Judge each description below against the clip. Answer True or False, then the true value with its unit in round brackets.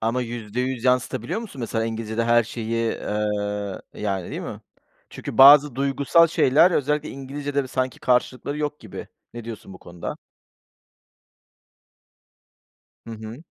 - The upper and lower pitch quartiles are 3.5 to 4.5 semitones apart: True (3.9 semitones)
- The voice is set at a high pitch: False (120 Hz)